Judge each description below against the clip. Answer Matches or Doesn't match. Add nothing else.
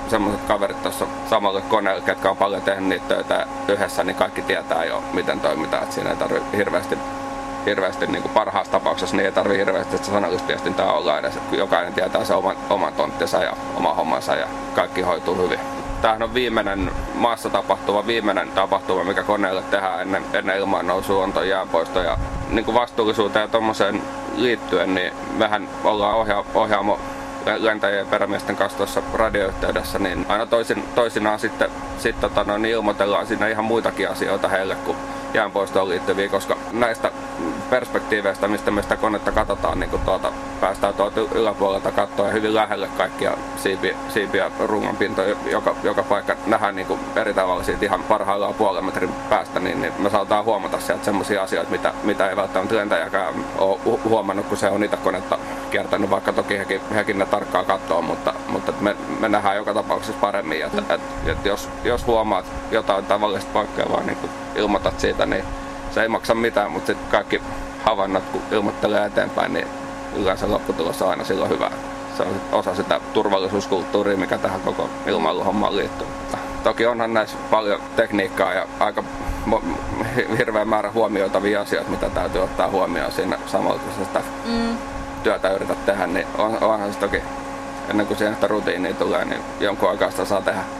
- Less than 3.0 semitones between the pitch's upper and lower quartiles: Matches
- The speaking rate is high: Matches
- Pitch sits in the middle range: Doesn't match